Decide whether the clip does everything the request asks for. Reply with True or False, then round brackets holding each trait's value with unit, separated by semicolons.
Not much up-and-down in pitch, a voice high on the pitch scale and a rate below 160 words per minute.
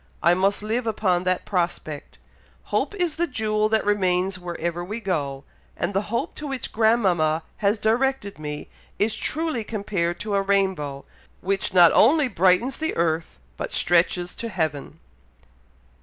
False (4.2 semitones; 195 Hz; 150 wpm)